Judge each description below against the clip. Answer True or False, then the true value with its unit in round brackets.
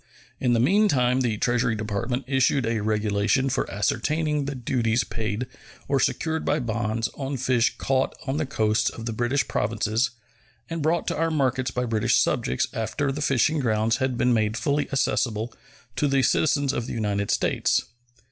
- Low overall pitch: True (125 Hz)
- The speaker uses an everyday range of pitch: True (3.7 semitones)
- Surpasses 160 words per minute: True (170 wpm)